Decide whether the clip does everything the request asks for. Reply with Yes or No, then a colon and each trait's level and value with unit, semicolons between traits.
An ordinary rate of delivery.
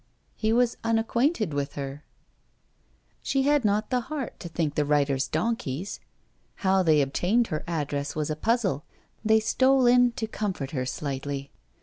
Yes: average, 150 wpm